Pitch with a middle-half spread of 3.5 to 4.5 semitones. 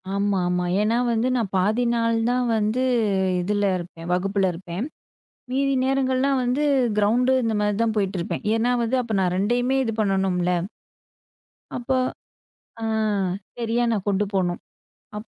Yes: average, 4.1 semitones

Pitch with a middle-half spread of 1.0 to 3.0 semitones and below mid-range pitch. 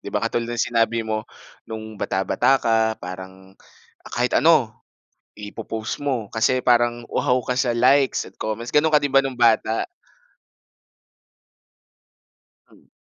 Yes: average, 2.7 semitones; low, 115 Hz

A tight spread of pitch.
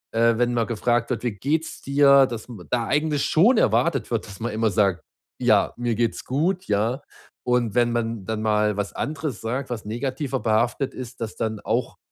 No: average, 3.6 semitones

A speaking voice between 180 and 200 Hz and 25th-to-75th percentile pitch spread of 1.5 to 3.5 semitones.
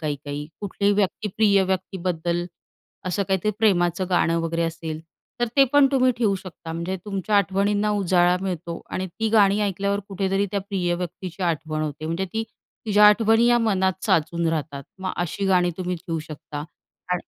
Yes: medium, 185 Hz; average, 3.1 semitones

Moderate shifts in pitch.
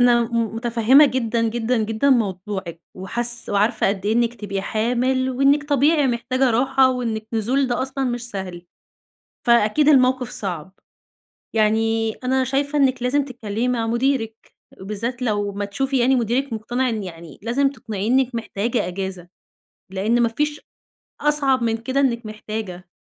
Yes: average, 3.3 semitones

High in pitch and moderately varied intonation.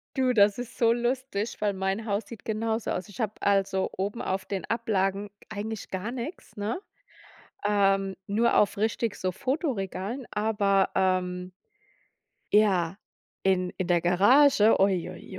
Yes: high, 205 Hz; average, 3.0 semitones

